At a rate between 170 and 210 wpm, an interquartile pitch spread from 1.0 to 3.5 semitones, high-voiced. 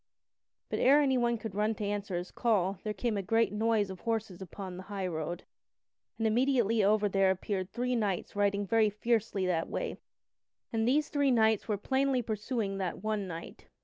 Yes: average, 180 wpm; average, 2.9 semitones; high, 210 Hz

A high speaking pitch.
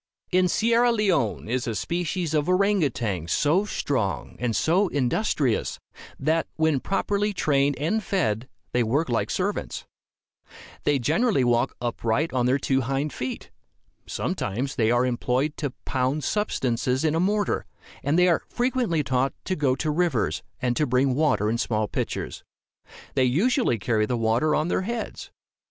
No: medium, 140 Hz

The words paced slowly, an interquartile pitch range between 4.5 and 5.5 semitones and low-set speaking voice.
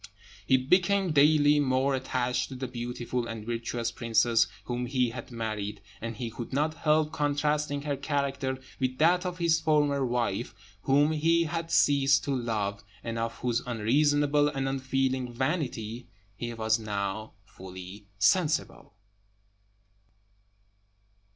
No: slow, 130 wpm; average, 4.0 semitones; low, 130 Hz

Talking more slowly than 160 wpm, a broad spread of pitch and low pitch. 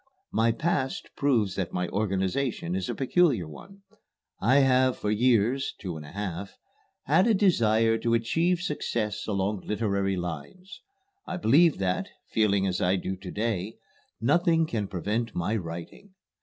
Yes: average, 150 wpm; wide, 6.0 semitones; low, 110 Hz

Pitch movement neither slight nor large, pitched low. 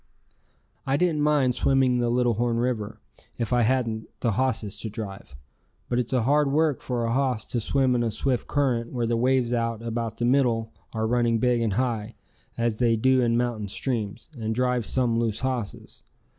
No: narrow, 2.2 semitones; low, 120 Hz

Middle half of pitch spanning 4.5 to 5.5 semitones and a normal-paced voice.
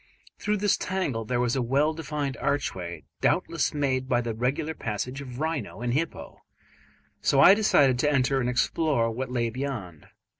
No: average, 3.7 semitones; average, 165 wpm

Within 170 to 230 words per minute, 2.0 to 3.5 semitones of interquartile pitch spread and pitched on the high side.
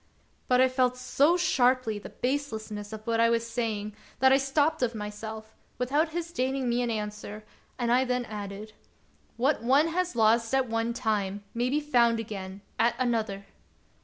Yes: average, 175 wpm; average, 3.2 semitones; high, 235 Hz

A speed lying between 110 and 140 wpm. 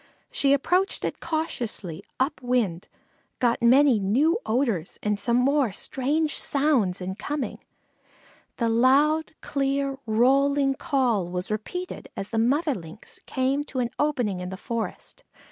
Yes: slow, 135 wpm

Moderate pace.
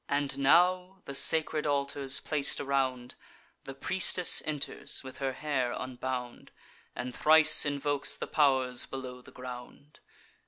No: slow, 125 wpm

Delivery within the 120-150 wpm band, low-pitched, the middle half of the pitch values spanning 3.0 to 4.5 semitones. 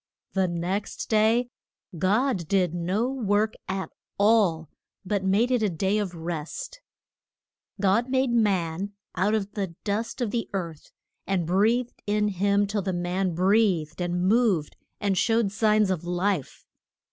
No: average, 145 wpm; high, 200 Hz; average, 3.5 semitones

